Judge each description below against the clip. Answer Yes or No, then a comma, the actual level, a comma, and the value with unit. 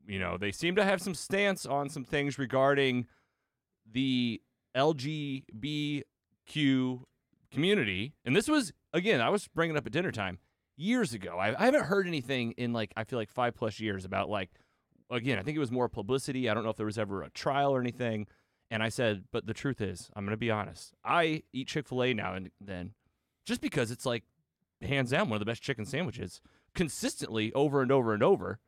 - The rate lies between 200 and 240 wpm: Yes, fast, 205 wpm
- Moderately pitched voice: No, low, 125 Hz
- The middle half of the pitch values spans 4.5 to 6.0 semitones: Yes, average, 5.1 semitones